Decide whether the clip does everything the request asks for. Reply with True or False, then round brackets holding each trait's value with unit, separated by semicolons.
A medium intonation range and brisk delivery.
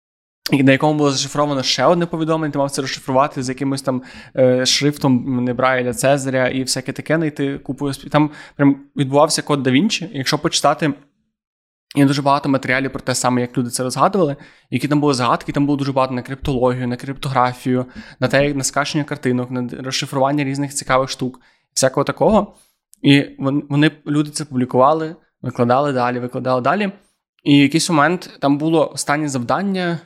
False (2.2 semitones; 170 wpm)